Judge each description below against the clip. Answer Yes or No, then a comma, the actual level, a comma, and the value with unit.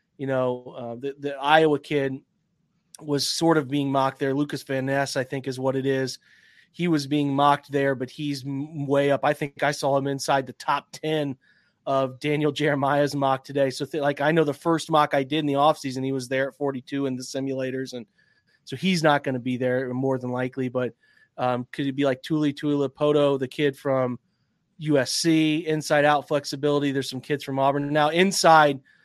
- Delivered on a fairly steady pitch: Yes, narrow, 1.9 semitones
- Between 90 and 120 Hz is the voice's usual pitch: No, medium, 140 Hz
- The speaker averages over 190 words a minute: Yes, average, 200 wpm